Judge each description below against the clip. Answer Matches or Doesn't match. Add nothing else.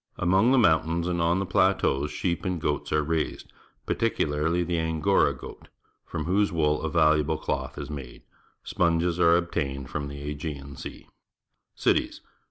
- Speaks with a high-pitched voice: Doesn't match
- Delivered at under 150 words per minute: Doesn't match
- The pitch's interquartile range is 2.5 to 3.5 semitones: Matches